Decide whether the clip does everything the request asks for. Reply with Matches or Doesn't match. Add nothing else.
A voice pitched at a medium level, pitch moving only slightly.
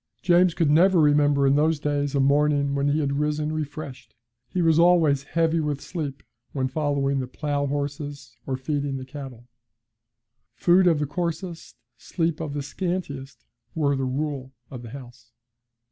Matches